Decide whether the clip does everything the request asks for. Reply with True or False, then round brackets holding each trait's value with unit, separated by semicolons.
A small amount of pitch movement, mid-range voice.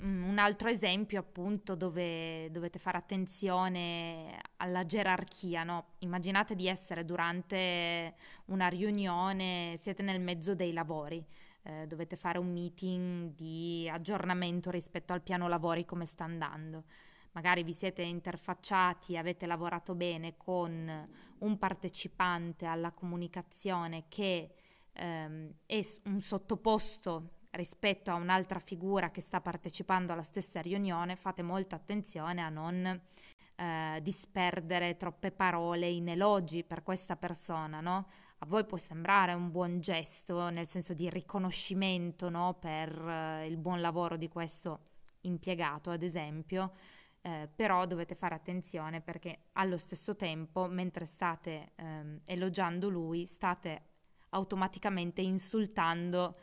True (1.8 semitones; 180 Hz)